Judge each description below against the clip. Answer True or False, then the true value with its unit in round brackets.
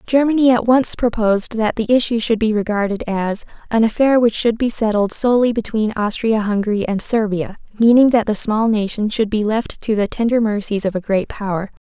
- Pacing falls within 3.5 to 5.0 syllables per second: False (5.4 syllables/s)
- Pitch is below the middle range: False (220 Hz)